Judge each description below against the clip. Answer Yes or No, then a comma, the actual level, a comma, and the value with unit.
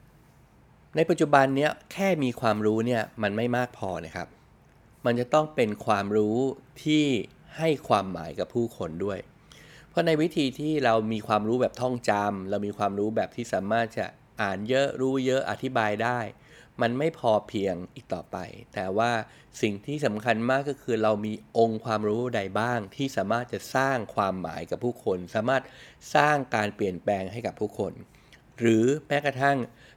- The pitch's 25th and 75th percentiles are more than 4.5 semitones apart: No, average, 4.0 semitones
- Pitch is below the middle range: Yes, low, 120 Hz